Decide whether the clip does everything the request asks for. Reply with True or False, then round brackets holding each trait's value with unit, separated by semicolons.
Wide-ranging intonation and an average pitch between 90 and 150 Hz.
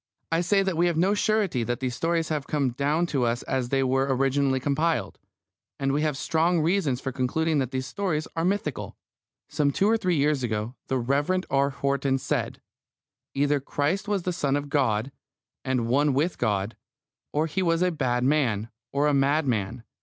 False (3.9 semitones; 140 Hz)